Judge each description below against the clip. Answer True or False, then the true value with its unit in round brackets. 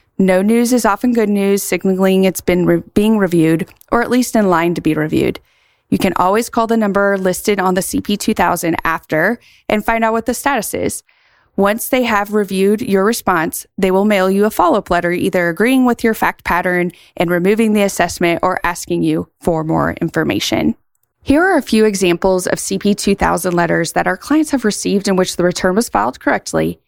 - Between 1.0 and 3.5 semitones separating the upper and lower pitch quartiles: False (3.9 semitones)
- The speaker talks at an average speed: True (195 wpm)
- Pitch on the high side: True (195 Hz)